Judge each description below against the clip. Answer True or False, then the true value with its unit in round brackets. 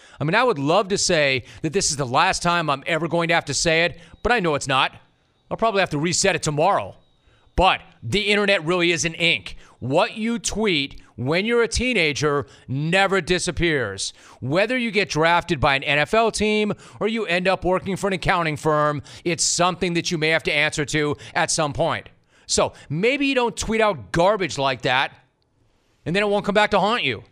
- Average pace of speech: False (210 wpm)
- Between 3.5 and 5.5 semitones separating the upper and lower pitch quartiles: True (5.0 semitones)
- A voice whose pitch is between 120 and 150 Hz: False (170 Hz)